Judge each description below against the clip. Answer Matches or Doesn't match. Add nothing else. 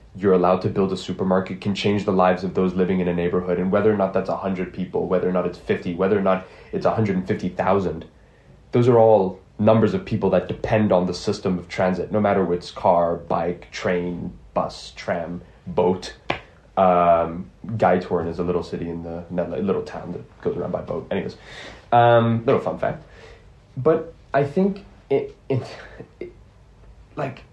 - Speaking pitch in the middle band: Doesn't match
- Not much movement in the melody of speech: Doesn't match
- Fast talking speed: Doesn't match